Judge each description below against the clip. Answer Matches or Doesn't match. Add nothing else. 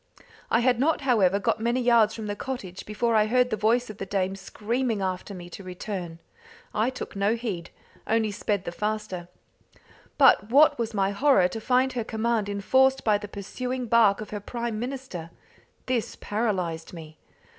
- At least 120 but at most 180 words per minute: Matches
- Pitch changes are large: Doesn't match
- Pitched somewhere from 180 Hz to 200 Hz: Doesn't match